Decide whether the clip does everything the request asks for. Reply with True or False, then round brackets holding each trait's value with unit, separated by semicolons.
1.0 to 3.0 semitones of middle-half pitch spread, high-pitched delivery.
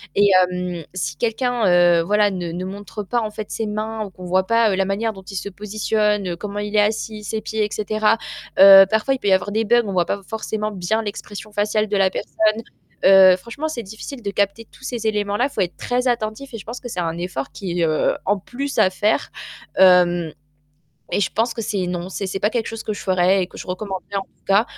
True (2.7 semitones; 205 Hz)